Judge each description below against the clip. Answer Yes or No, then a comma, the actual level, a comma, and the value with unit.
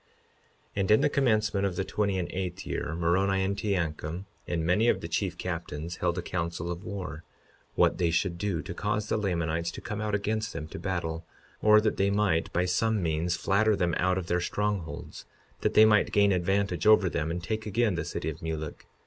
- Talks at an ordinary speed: No, fast, 210 wpm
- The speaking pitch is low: Yes, very low, 95 Hz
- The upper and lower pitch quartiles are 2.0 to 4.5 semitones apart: Yes, average, 3.5 semitones